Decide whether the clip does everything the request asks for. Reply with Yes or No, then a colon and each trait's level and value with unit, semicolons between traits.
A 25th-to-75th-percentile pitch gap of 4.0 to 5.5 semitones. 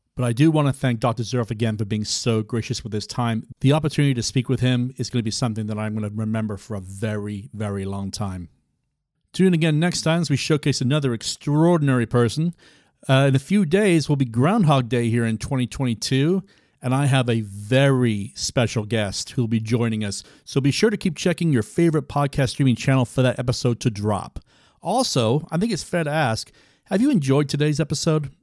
Yes: average, 5.1 semitones